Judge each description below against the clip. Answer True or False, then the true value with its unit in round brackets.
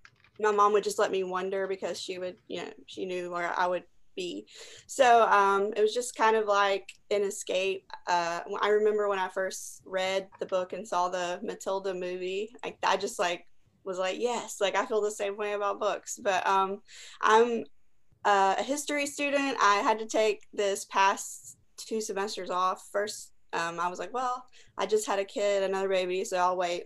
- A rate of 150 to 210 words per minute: True (195 wpm)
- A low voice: False (200 Hz)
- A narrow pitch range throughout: True (2.3 semitones)